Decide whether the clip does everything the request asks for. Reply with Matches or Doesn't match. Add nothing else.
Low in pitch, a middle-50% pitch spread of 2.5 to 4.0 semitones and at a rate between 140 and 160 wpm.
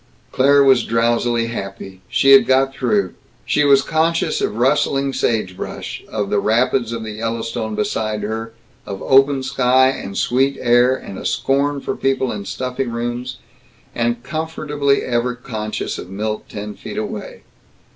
Matches